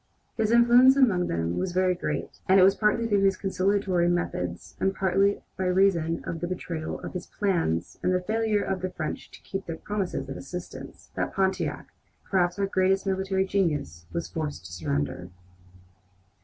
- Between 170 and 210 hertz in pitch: Yes, medium, 185 Hz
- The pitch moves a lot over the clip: No, average, 2.8 semitones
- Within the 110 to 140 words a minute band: No, average, 175 wpm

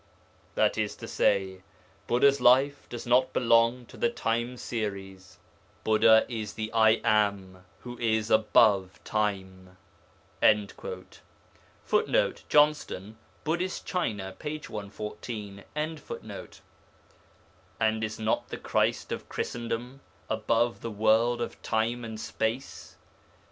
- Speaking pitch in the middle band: No, low, 110 Hz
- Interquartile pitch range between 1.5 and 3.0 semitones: Yes, narrow, 2.6 semitones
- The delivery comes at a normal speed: No, slow, 105 wpm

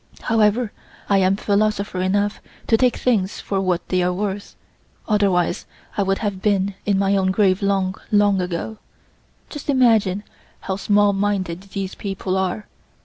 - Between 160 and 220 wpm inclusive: No, average, 150 wpm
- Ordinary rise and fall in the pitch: No, narrow, 1.7 semitones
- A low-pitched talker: No, high, 200 Hz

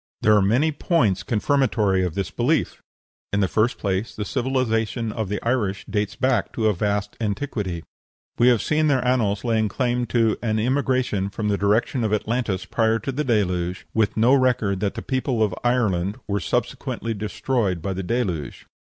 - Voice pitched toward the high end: No, low, 110 Hz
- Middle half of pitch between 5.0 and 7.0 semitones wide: No, average, 3.7 semitones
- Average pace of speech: Yes, average, 175 wpm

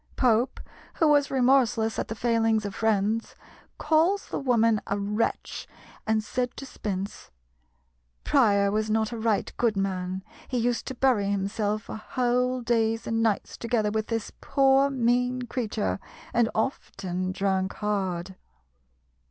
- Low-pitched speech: No, high, 225 Hz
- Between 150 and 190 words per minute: No, average, 140 wpm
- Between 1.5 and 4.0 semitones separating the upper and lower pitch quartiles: Yes, average, 3.3 semitones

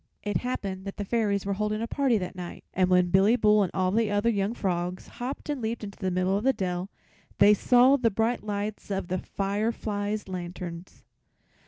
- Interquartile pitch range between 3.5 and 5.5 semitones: No, average, 3.0 semitones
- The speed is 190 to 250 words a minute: Yes, average, 200 wpm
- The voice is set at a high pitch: Yes, high, 205 Hz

